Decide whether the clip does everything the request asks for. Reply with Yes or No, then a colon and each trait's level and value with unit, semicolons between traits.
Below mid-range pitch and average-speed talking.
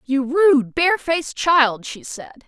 No: very high, 290 Hz; average, 145 wpm